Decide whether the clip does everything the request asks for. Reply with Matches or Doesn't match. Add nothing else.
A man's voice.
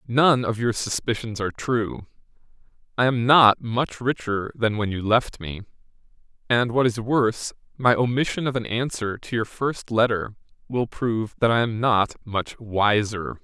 Matches